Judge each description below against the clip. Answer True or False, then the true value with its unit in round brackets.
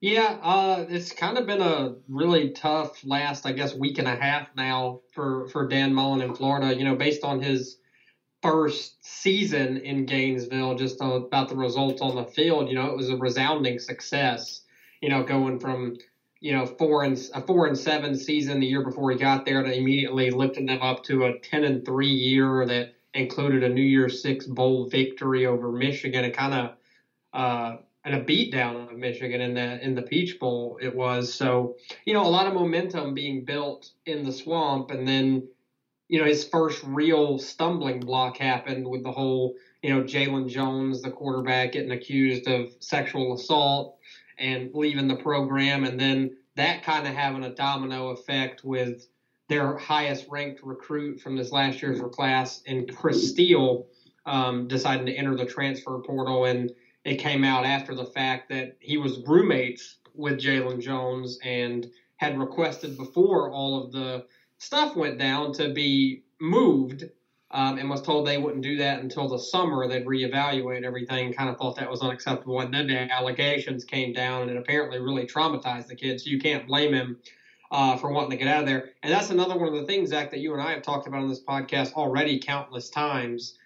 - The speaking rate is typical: True (190 wpm)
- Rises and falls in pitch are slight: True (2.0 semitones)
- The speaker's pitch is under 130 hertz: False (135 Hz)